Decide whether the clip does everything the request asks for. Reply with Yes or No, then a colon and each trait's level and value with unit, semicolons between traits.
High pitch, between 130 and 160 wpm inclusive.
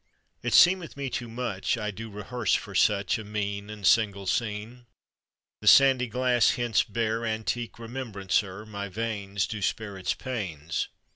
No: low, 110 Hz; average, 150 wpm